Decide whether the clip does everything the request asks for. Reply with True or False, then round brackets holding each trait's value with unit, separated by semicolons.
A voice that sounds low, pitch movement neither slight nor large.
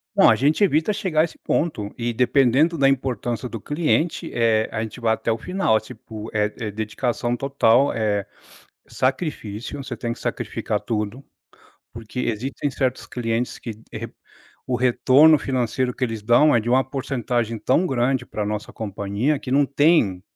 True (125 Hz; 3.7 semitones)